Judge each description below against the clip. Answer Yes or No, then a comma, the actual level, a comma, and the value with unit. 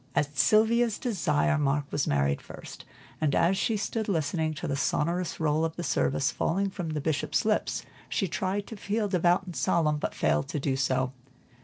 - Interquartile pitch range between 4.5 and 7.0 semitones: Yes, average, 5.1 semitones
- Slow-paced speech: No, average, 185 wpm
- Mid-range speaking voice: Yes, medium, 165 Hz